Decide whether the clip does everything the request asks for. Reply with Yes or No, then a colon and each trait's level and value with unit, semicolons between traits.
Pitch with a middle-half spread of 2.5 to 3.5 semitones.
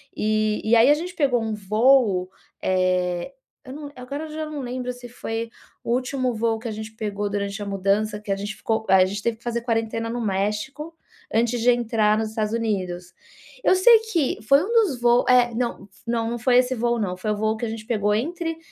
Yes: average, 3.0 semitones